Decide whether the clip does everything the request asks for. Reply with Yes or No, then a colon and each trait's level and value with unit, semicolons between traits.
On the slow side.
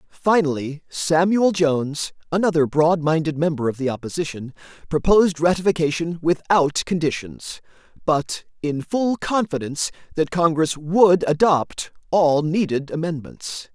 Yes: slow, 110 wpm